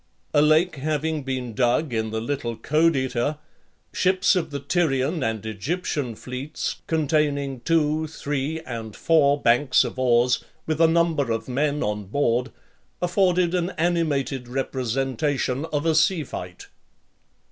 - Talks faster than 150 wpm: No, slow, 135 wpm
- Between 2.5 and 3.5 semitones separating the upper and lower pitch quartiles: No, average, 4.3 semitones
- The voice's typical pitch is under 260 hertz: Yes, medium, 140 Hz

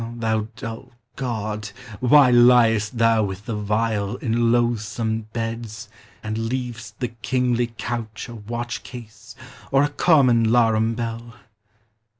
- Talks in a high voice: No, low, 115 Hz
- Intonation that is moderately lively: No, narrow, 1.6 semitones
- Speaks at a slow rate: Yes, slow, 130 wpm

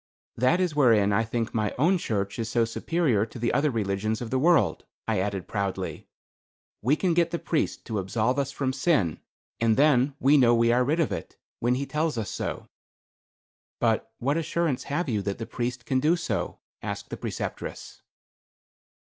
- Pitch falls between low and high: No, low, 125 Hz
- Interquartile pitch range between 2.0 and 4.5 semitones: No, average, 5.1 semitones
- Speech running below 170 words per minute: No, average, 185 wpm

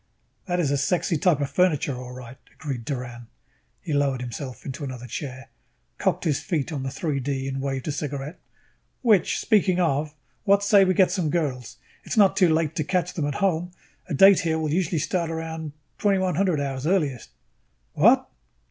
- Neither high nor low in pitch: Yes, medium, 150 Hz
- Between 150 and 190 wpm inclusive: Yes, average, 185 wpm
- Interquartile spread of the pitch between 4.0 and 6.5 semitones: Yes, average, 4.7 semitones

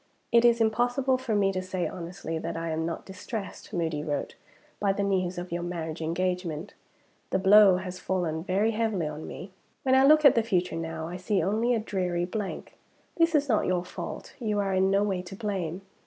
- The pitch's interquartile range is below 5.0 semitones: Yes, average, 3.7 semitones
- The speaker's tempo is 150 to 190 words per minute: No, fast, 205 wpm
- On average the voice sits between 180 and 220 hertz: Yes, high, 190 Hz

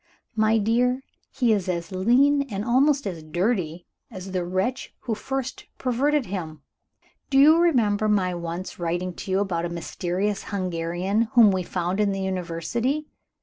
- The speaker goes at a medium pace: Yes, average, 155 wpm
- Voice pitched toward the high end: Yes, high, 200 Hz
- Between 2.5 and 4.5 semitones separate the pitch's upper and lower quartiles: No, average, 5.3 semitones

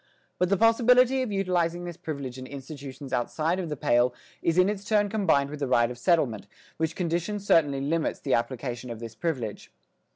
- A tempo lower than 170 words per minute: No, average, 190 wpm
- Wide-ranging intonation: Yes, wide, 6.0 semitones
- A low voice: No, medium, 160 Hz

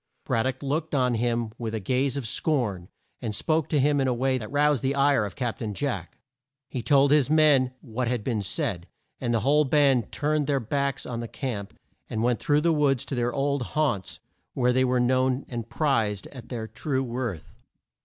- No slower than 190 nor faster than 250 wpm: Yes, fast, 205 wpm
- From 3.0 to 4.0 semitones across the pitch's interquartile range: Yes, average, 3.4 semitones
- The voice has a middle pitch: No, low, 130 Hz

